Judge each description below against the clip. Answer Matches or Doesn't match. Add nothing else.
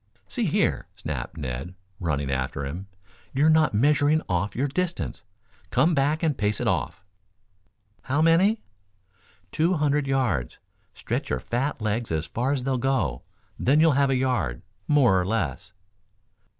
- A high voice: Doesn't match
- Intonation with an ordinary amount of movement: Doesn't match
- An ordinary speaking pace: Matches